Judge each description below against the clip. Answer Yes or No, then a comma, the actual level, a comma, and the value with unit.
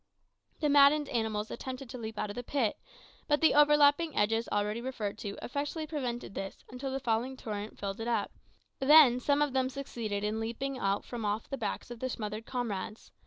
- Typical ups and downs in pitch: Yes, average, 4.4 semitones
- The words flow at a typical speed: Yes, average, 195 wpm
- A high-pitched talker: Yes, high, 245 Hz